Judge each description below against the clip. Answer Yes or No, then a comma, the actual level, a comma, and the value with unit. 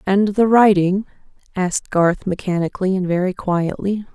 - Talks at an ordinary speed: No, slow, 130 wpm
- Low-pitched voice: No, high, 190 Hz